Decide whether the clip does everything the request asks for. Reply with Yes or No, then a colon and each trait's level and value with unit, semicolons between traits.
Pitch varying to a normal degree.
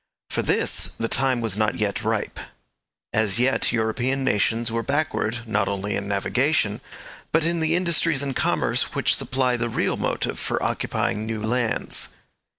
Yes: average, 3.7 semitones